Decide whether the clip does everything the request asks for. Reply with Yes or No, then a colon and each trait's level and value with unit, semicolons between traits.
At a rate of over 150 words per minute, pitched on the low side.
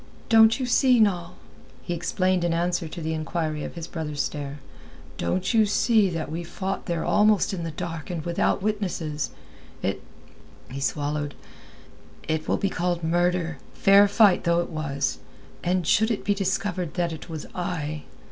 No: average, 165 wpm; medium, 175 Hz